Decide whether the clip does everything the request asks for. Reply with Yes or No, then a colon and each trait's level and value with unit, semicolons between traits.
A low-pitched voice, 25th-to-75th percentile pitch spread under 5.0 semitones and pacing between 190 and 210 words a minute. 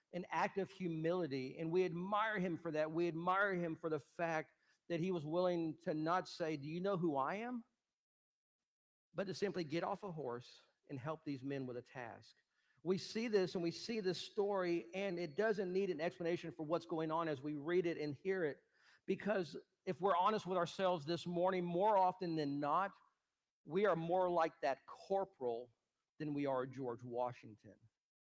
No: medium, 170 Hz; average, 3.5 semitones; average, 195 wpm